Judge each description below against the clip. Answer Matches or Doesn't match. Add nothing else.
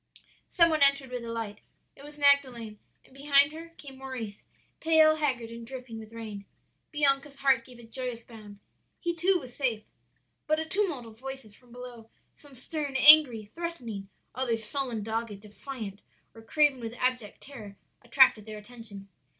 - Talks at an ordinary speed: Matches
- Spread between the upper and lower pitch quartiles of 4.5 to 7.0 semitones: Doesn't match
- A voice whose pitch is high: Matches